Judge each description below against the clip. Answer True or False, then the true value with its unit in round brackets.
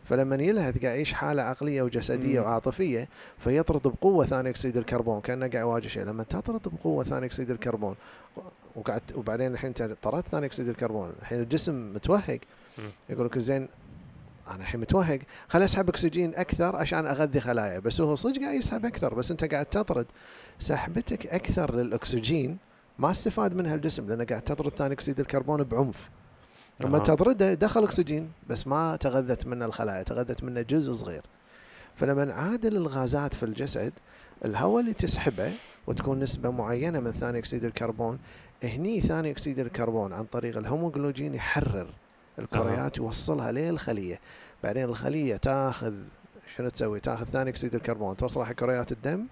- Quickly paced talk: True (145 wpm)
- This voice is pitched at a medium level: False (130 Hz)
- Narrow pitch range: False (4.5 semitones)